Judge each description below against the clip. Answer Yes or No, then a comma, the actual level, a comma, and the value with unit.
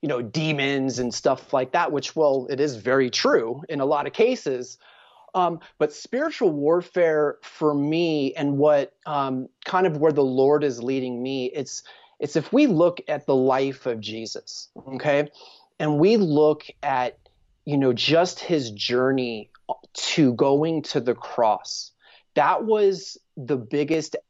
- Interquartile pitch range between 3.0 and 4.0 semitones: Yes, average, 3.3 semitones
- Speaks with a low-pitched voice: No, medium, 145 Hz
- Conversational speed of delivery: Yes, average, 160 wpm